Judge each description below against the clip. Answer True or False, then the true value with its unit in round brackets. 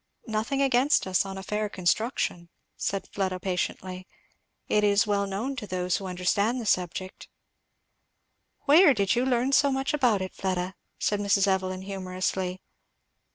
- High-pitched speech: True (200 Hz)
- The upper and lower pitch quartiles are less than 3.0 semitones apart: False (4.1 semitones)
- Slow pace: False (150 wpm)